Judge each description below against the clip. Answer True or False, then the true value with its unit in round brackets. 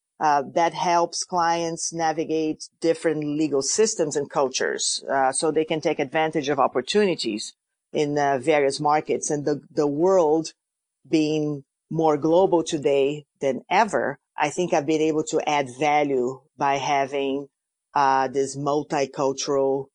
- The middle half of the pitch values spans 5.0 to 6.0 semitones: False (2.6 semitones)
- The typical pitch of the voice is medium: True (150 Hz)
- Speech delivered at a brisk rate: False (135 wpm)